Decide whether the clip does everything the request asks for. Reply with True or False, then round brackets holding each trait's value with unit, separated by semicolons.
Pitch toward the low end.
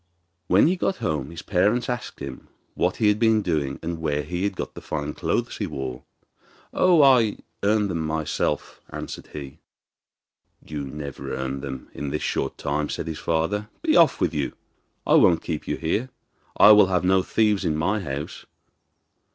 True (85 Hz)